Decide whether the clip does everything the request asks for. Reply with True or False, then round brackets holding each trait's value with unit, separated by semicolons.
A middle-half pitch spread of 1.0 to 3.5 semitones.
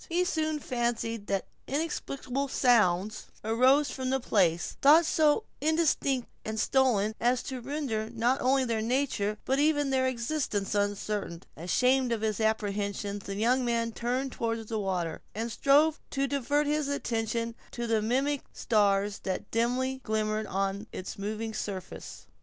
False (4.2 semitones)